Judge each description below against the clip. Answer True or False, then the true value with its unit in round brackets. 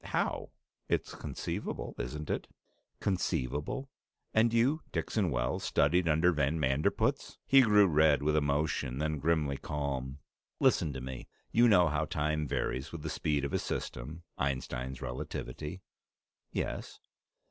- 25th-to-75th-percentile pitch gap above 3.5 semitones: True (3.9 semitones)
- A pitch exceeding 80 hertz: False (75 Hz)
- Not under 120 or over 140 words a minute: True (135 wpm)